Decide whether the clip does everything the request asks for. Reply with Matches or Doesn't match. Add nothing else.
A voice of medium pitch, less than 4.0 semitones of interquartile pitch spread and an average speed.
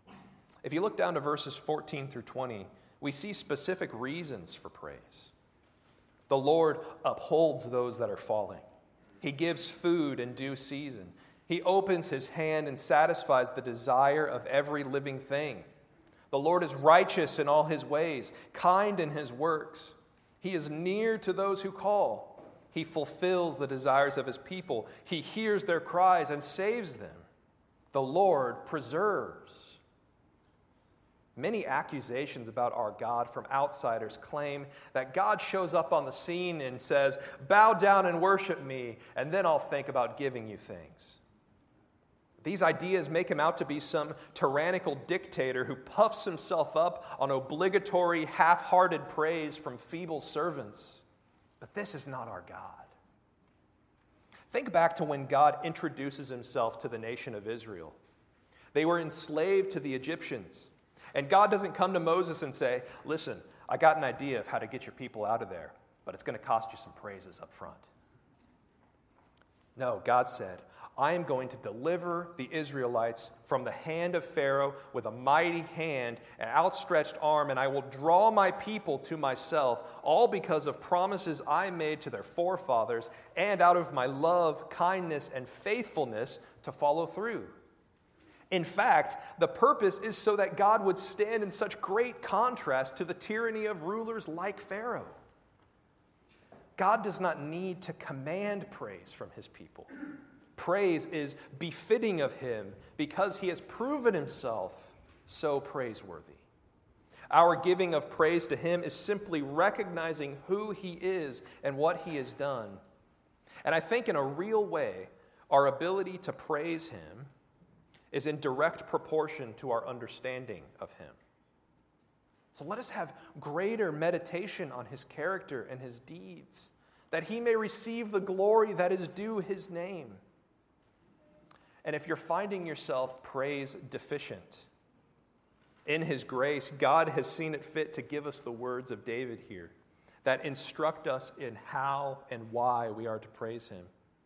Doesn't match